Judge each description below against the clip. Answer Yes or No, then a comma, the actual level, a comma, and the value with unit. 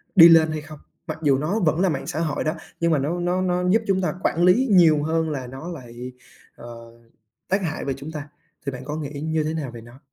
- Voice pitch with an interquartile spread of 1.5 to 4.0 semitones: Yes, average, 3.7 semitones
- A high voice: No, medium, 155 Hz